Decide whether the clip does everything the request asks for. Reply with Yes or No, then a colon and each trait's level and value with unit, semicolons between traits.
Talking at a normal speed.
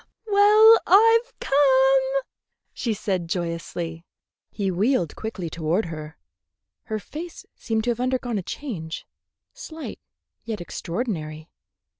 No: slow, 110 wpm